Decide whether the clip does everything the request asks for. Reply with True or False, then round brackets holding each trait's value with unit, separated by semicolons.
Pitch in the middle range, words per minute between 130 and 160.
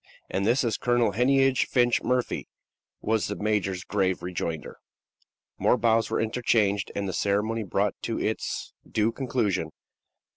False (110 Hz; 140 wpm)